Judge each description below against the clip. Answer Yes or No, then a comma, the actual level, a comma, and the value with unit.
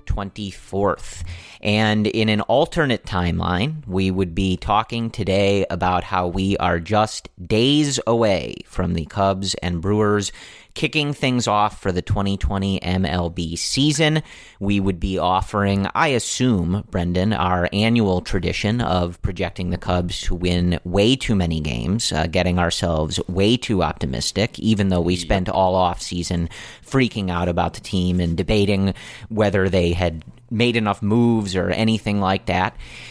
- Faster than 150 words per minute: No, average, 145 wpm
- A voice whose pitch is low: Yes, very low, 95 Hz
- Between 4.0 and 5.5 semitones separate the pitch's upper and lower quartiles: No, average, 3.2 semitones